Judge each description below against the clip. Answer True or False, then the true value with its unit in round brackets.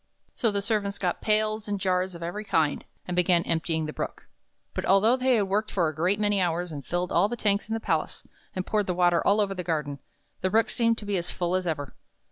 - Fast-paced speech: True (240 wpm)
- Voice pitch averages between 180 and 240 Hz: True (185 Hz)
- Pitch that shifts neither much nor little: True (3.5 semitones)